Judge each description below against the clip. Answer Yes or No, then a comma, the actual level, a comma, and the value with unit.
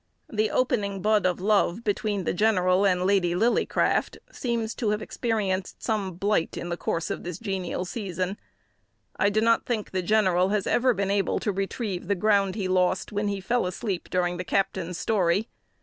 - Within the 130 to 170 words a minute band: No, average, 180 wpm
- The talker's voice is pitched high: Yes, high, 195 Hz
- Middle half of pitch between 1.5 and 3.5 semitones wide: Yes, average, 2.8 semitones